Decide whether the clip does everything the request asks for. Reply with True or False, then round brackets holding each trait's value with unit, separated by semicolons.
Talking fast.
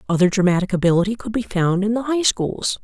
True (210 wpm)